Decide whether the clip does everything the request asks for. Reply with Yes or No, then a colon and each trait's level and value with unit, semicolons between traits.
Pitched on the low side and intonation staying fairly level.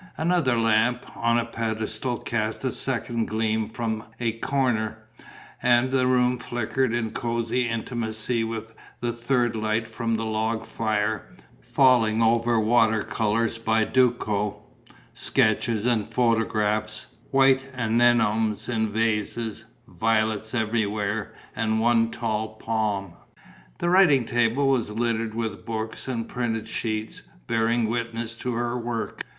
Yes: low, 115 Hz; narrow, 1.6 semitones